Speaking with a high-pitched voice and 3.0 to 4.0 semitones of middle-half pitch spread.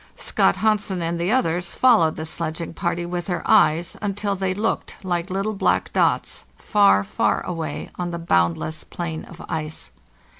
No: medium, 175 Hz; average, 3.3 semitones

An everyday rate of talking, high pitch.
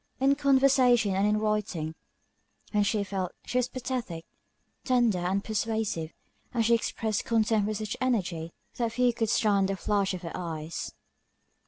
Yes: average, 155 wpm; high, 215 Hz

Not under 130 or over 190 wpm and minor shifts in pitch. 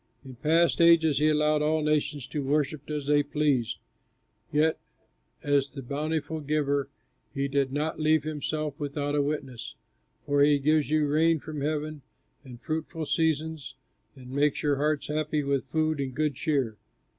Yes: average, 155 wpm; narrow, 1.6 semitones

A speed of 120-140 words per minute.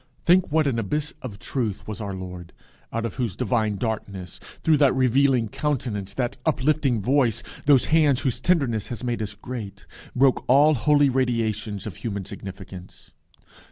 No: average, 155 wpm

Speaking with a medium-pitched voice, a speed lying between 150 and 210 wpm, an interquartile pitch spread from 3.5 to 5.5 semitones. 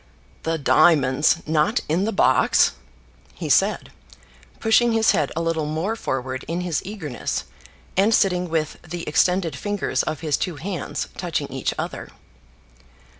No: medium, 165 Hz; average, 140 wpm; average, 4.3 semitones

